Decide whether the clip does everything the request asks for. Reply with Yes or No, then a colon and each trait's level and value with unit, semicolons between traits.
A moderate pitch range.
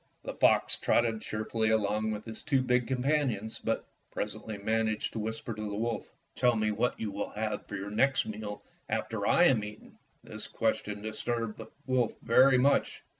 No: narrow, 2.2 semitones